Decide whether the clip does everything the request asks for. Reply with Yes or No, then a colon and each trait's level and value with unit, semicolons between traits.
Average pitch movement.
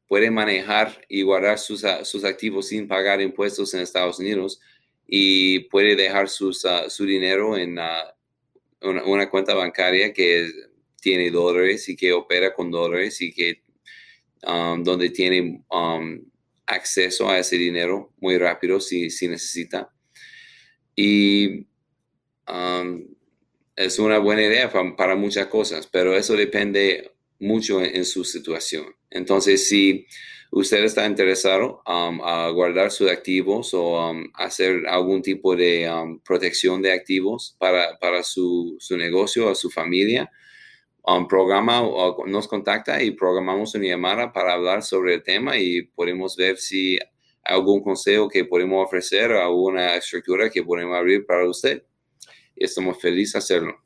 No: narrow, 1.7 semitones